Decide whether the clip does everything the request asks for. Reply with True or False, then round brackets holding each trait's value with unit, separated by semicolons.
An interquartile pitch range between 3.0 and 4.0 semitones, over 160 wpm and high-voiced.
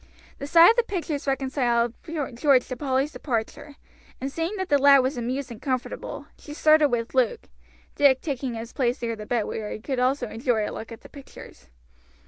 True (3.4 semitones; 190 wpm; 265 Hz)